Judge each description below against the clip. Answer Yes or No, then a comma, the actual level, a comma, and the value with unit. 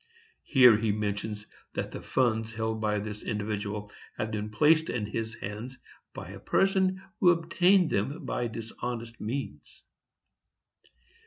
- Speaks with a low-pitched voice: Yes, low, 110 Hz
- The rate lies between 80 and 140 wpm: Yes, slow, 135 wpm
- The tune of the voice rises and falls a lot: No, average, 4.5 semitones